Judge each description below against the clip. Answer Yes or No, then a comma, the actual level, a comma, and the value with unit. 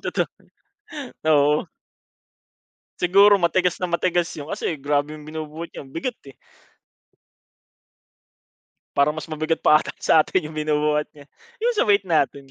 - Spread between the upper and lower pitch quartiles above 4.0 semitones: No, average, 2.8 semitones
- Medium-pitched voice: Yes, medium, 155 Hz